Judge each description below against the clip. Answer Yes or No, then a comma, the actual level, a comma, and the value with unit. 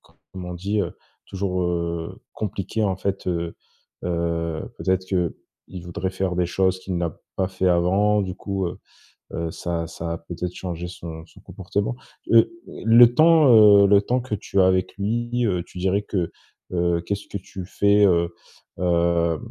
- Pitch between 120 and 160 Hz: No, very low, 95 Hz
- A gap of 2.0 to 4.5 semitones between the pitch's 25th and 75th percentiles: Yes, average, 2.8 semitones